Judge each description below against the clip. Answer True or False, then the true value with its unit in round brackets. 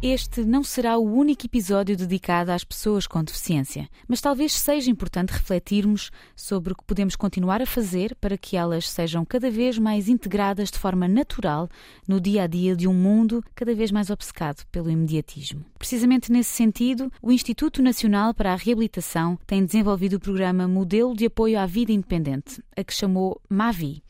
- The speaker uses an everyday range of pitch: True (4.4 semitones)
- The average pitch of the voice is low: False (205 Hz)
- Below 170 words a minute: False (175 wpm)